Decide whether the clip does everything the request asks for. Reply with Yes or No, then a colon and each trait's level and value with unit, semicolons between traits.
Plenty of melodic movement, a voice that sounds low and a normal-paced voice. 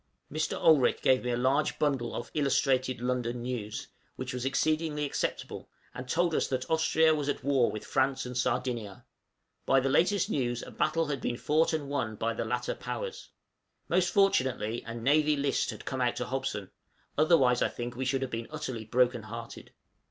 No: average, 3.6 semitones; low, 130 Hz; average, 180 wpm